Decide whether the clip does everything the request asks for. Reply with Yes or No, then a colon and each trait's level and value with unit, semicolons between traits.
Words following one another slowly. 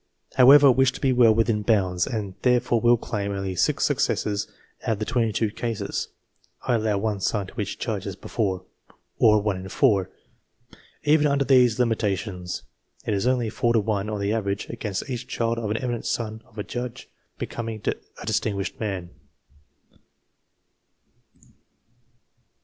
No: average, 165 wpm